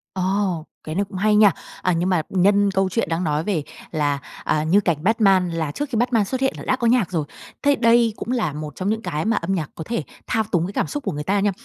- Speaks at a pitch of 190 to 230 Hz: Yes, high, 195 Hz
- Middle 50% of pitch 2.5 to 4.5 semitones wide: No, average, 5.1 semitones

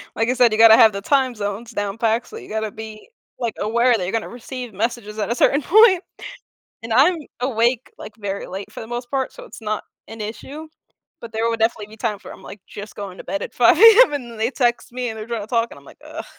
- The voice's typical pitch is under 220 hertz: No, high, 230 Hz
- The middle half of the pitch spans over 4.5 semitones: No, average, 2.7 semitones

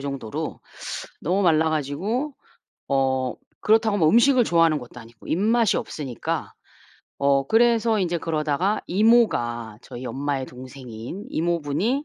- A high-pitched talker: No, medium, 160 Hz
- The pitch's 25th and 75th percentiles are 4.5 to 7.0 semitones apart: No, wide, 8.1 semitones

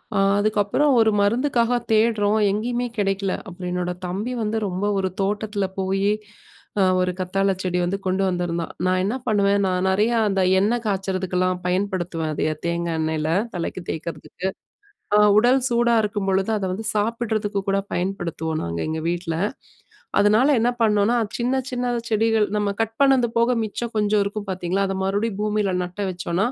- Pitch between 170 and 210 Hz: Yes, high, 200 Hz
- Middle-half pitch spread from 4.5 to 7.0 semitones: No, average, 3.0 semitones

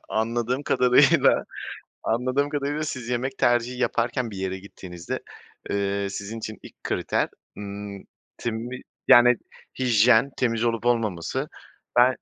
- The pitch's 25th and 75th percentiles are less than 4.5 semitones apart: Yes, average, 3.7 semitones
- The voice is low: Yes, low, 120 Hz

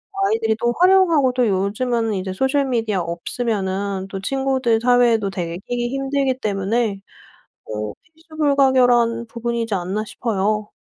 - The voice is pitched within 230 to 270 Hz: Yes, high, 235 Hz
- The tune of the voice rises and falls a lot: No, average, 4.9 semitones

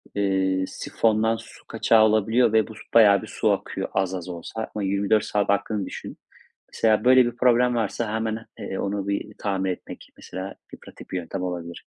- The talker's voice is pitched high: No, low, 105 Hz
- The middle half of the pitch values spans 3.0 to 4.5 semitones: No, narrow, 2.6 semitones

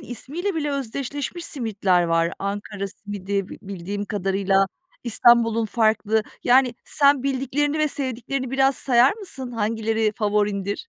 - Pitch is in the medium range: No, high, 225 Hz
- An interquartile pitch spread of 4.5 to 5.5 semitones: Yes, average, 4.9 semitones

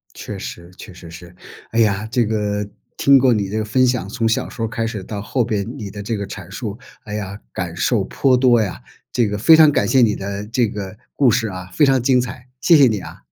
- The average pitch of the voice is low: Yes, low, 110 Hz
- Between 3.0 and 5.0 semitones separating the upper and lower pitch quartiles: Yes, average, 3.6 semitones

